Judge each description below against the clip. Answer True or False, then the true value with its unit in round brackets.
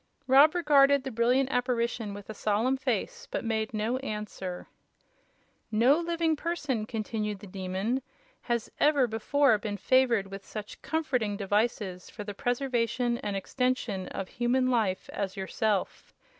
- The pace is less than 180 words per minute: True (140 wpm)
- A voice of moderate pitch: False (235 Hz)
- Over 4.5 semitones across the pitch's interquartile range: False (4.2 semitones)